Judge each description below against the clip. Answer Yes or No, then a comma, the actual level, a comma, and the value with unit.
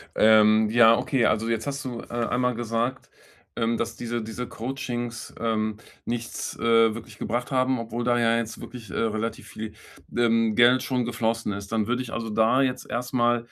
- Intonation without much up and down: Yes, narrow, 1.5 semitones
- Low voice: Yes, low, 115 Hz